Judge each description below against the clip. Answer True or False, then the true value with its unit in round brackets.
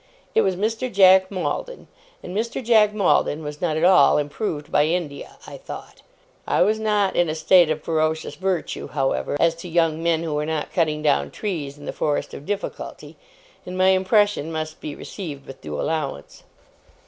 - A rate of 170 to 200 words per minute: True (180 wpm)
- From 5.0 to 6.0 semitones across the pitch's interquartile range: False (4.2 semitones)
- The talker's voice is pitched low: False (165 Hz)